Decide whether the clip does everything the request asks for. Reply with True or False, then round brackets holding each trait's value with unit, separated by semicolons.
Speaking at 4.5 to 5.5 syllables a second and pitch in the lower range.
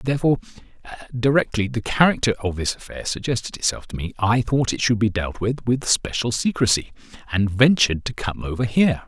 False (5.8 syllables/s; 115 Hz)